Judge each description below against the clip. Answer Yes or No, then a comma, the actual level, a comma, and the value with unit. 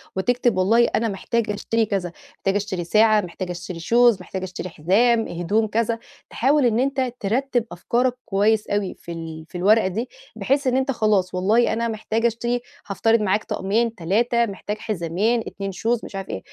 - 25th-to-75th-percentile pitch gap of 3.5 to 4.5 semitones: Yes, average, 3.8 semitones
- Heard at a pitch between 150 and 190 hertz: No, high, 215 Hz